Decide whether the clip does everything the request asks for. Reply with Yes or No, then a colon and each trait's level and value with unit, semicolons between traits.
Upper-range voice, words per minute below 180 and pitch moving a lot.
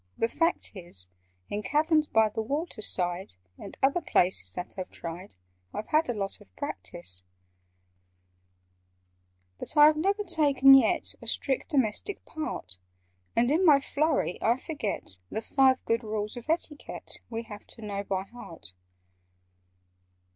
Yes: high, 230 Hz; average, 145 wpm; wide, 7.3 semitones